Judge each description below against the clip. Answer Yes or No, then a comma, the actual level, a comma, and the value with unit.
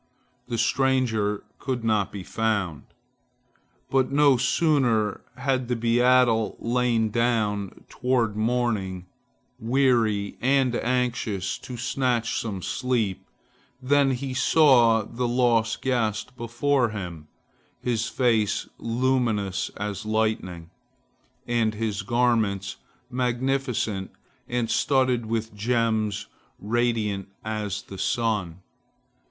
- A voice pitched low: Yes, low, 115 Hz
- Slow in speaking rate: Yes, slow, 100 wpm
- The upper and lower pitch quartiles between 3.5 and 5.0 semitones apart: No, average, 3.1 semitones